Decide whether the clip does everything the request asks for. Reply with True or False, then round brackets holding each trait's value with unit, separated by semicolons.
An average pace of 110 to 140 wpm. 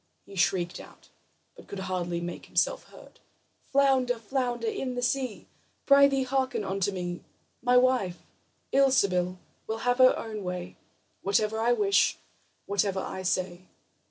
True (135 wpm)